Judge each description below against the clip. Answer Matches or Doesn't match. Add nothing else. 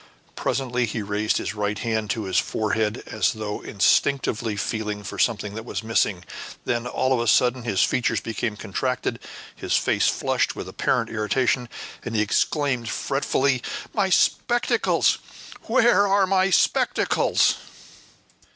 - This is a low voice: Matches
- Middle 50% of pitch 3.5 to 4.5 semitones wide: Matches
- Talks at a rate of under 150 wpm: Matches